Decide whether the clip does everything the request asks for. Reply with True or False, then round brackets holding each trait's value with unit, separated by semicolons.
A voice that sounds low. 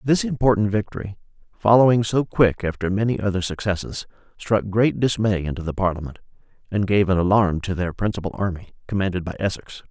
True (100 Hz)